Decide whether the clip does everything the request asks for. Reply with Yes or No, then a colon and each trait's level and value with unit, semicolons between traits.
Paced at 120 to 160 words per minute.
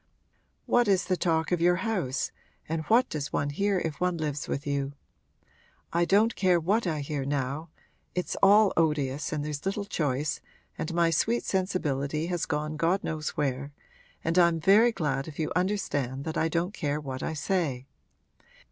No: average, 175 wpm